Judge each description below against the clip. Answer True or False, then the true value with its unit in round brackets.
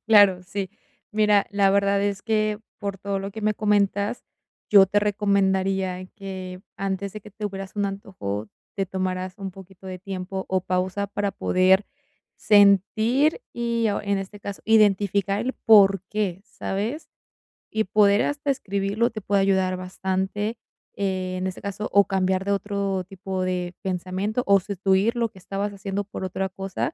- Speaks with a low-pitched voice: False (195 Hz)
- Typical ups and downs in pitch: False (1.5 semitones)